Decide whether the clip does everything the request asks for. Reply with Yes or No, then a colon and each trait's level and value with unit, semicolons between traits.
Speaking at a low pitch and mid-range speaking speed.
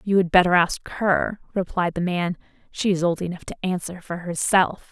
No: medium, 180 Hz; average, 195 wpm